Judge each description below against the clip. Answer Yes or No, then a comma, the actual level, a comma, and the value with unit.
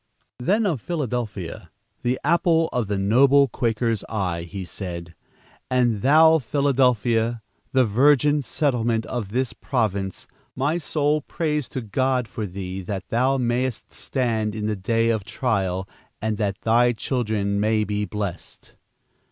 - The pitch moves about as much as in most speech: Yes, average, 4.2 semitones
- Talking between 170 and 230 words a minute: No, slow, 135 wpm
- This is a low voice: Yes, low, 115 Hz